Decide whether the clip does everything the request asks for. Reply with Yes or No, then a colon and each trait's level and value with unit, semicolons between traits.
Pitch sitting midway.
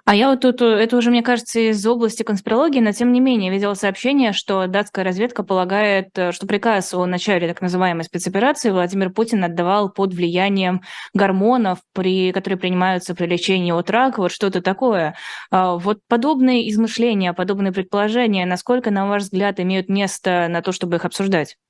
No: high, 195 Hz